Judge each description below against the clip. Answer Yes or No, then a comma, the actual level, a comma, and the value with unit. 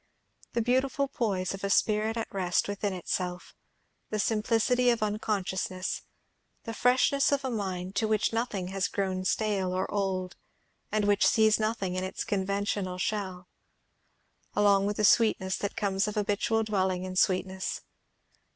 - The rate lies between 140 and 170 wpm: Yes, average, 150 wpm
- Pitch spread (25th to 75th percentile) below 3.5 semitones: Yes, average, 2.7 semitones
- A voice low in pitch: No, high, 200 Hz